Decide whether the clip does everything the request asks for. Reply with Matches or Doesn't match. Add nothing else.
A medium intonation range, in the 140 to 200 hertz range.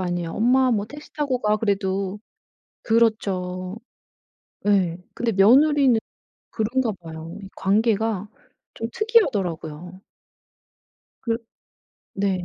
Doesn't match